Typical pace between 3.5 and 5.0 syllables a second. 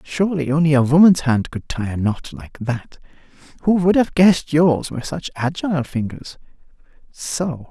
Yes: 4.9 syllables/s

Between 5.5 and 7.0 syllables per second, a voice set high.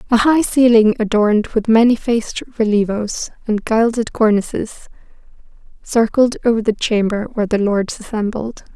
No: 4.9 syllables/s; high, 220 Hz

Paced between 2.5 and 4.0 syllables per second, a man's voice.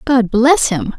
No: 3.4 syllables/s; female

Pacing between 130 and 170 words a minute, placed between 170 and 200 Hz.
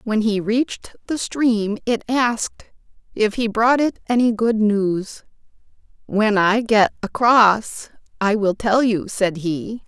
No: average, 145 wpm; high, 220 Hz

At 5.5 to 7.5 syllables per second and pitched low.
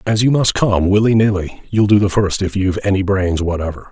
Yes: 5.7 syllables/s; low, 100 Hz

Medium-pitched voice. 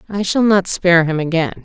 Yes: medium, 180 Hz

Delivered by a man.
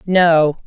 No: female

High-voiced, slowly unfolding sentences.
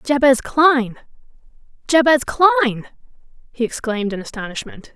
Yes: very high, 255 Hz; slow, 85 wpm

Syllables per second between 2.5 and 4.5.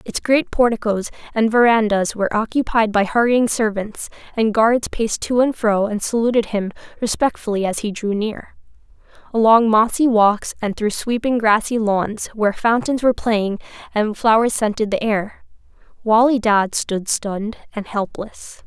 No: 4.7 syllables/s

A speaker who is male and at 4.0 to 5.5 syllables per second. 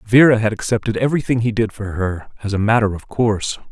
No: male; 6.2 syllables/s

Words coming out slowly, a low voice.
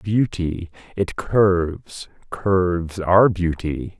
Yes: slow, 90 wpm; very low, 90 Hz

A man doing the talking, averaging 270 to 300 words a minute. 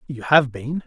No: male; fast, 210 wpm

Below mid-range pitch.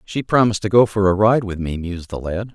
Yes: low, 100 Hz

